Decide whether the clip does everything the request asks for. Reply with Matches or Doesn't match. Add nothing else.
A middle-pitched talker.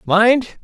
Doesn't match